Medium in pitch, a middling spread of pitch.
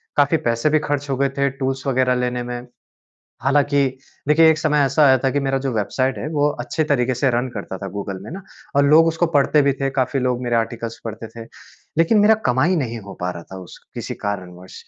No: low, 130 Hz; average, 3.8 semitones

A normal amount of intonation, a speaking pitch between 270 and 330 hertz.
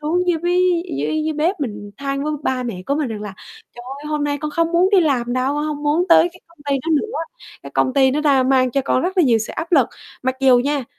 Yes: average, 4.3 semitones; very high, 290 Hz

